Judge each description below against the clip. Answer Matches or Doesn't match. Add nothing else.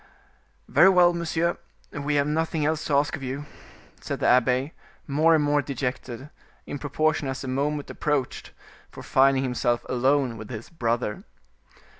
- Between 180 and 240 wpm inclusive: Doesn't match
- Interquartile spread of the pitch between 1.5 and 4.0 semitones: Matches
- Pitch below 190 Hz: Matches